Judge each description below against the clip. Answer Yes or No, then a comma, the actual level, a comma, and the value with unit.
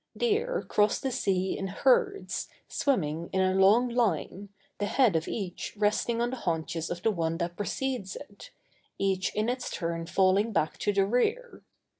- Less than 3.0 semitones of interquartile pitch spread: No, wide, 5.4 semitones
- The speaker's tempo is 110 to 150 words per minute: No, average, 170 wpm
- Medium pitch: No, high, 205 Hz